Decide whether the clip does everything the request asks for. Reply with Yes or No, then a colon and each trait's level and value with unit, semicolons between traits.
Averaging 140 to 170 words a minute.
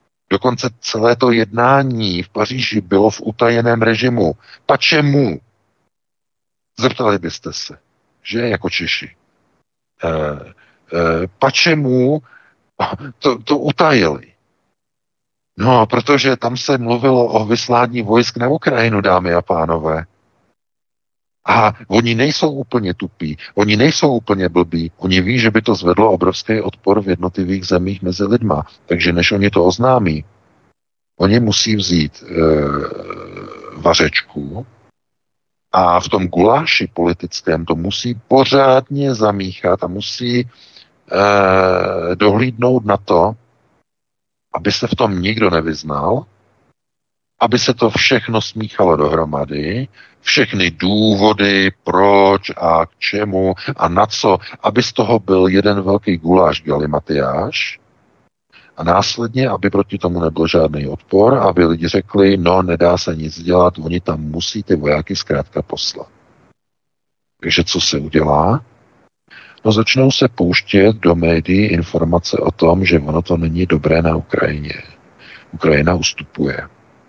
No: average, 120 wpm